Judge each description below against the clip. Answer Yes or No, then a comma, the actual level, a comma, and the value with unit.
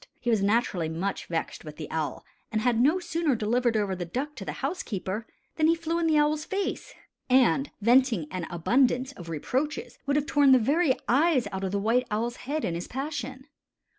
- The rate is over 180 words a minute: Yes, average, 200 wpm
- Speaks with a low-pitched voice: No, very high, 250 Hz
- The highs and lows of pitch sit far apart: Yes, wide, 6.6 semitones